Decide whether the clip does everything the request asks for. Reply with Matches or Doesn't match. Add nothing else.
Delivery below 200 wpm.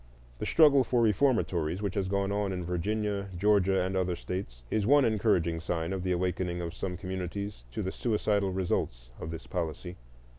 Matches